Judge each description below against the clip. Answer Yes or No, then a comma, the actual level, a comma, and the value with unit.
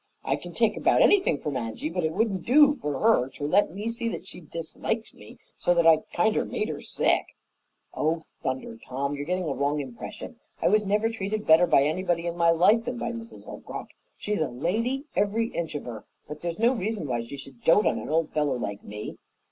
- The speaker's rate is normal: No, fast, 220 wpm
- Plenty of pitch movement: Yes, wide, 7.0 semitones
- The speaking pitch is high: No, medium, 170 Hz